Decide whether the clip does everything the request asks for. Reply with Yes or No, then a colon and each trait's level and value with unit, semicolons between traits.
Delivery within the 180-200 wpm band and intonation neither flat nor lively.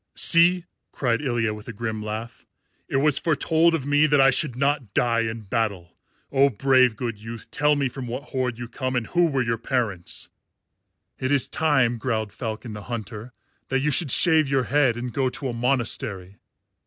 Yes: average, 190 wpm; average, 3.5 semitones